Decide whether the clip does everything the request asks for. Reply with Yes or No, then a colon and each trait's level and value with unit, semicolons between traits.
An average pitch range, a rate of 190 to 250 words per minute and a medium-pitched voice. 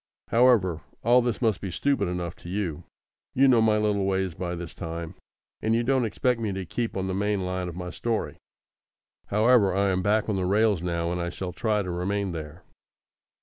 No: average, 3.8 semitones; fast, 205 wpm; very low, 95 Hz